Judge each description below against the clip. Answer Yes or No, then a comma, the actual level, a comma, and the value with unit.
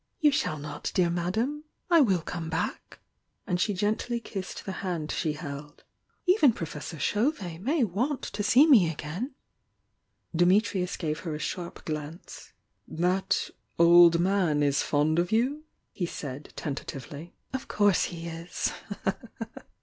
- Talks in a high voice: No, medium, 175 Hz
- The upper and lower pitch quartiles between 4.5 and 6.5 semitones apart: Yes, average, 5.1 semitones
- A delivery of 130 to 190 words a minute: Yes, average, 140 wpm